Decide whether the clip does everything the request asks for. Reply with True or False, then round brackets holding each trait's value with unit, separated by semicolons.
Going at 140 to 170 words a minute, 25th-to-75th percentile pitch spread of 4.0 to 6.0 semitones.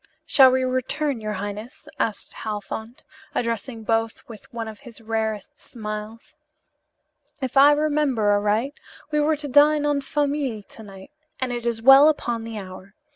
True (155 wpm; 4.6 semitones)